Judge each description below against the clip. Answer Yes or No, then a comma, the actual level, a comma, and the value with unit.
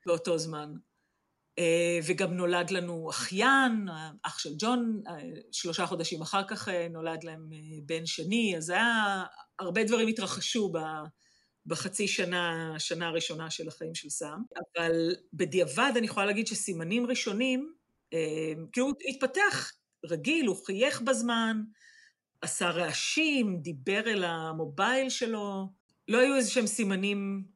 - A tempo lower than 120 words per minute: No, average, 125 wpm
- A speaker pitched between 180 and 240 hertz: Yes, high, 190 Hz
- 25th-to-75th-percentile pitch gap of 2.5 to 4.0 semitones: No, average, 5.3 semitones